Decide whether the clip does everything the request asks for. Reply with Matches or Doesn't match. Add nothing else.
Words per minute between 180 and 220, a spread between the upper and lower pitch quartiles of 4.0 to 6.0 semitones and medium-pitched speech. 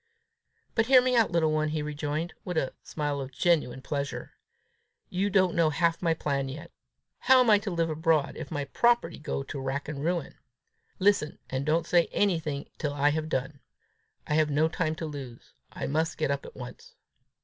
Doesn't match